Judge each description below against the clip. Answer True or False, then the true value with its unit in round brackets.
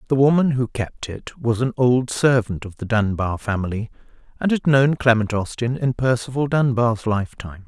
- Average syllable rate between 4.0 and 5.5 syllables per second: True (5.0 syllables/s)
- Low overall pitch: True (120 Hz)